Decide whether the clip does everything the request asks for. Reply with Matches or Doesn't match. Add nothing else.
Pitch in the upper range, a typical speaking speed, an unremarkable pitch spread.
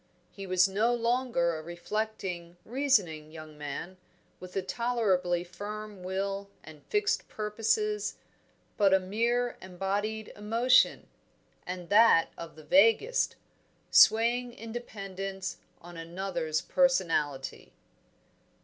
Doesn't match